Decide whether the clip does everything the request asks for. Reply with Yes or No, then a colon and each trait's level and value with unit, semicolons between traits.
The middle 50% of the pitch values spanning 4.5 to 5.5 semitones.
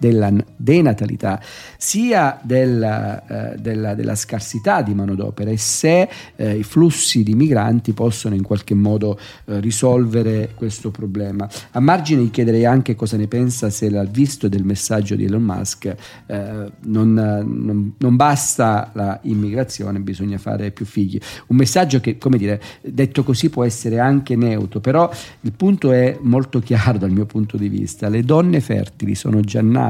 No: average, 3.6 semitones